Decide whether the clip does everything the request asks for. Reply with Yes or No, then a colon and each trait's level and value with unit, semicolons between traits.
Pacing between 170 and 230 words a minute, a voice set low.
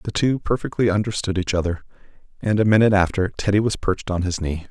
Yes: fast, 205 wpm; low, 100 Hz